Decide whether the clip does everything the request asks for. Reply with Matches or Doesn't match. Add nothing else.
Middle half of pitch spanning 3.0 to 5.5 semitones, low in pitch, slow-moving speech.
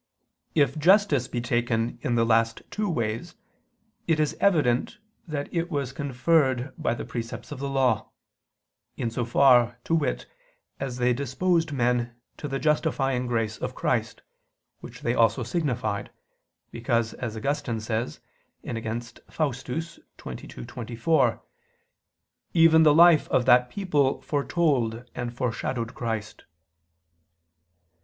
Matches